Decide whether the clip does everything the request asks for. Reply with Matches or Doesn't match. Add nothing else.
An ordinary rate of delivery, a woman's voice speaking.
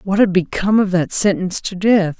Doesn't match